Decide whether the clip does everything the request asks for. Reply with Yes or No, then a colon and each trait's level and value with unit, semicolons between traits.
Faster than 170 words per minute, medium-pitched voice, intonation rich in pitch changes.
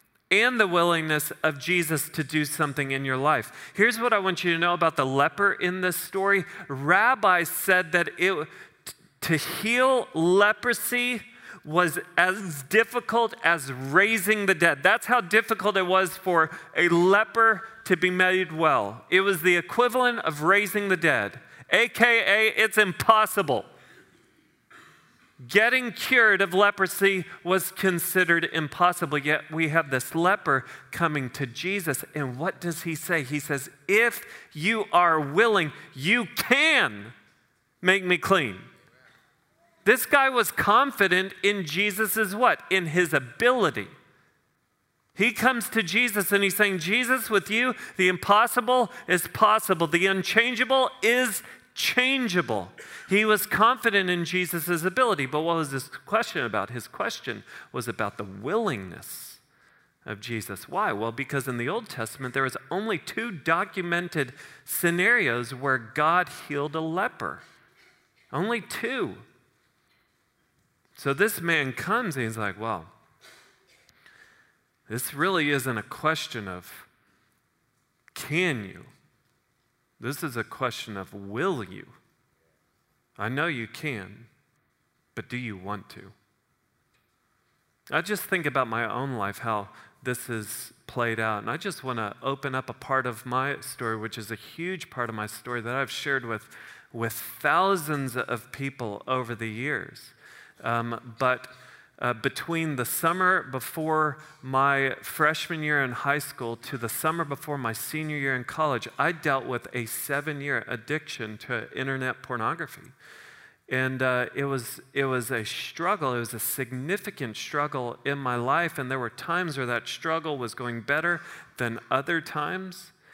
No: average, 145 wpm; medium, 155 Hz; wide, 6.8 semitones